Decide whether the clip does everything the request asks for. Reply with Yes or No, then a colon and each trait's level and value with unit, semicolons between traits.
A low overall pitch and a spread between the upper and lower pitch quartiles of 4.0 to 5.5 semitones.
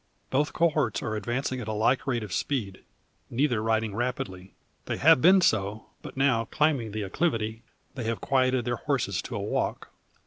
No: low, 120 Hz; average, 3.6 semitones